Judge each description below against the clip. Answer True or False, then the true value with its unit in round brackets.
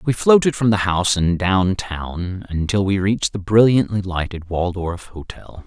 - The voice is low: True (95 Hz)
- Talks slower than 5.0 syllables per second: True (4.5 syllables/s)